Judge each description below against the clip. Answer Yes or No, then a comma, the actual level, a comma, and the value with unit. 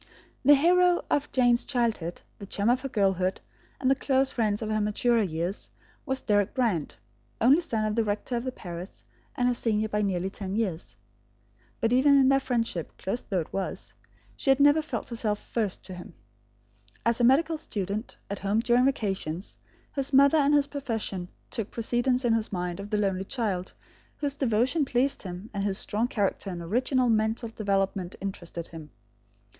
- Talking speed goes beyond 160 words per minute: Yes, average, 180 wpm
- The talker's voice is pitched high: Yes, high, 225 Hz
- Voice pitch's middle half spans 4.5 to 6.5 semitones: Yes, average, 4.9 semitones